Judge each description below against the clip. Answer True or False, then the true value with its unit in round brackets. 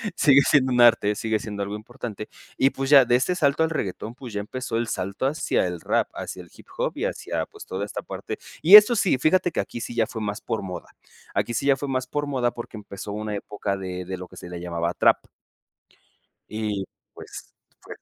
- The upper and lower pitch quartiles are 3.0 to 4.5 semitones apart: False (4.9 semitones)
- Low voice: True (115 Hz)